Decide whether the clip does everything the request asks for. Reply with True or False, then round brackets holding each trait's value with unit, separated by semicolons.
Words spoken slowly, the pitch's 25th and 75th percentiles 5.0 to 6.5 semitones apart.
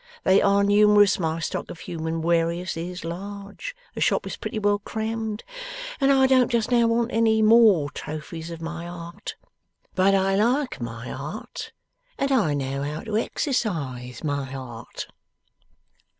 False (150 wpm; 5.4 semitones)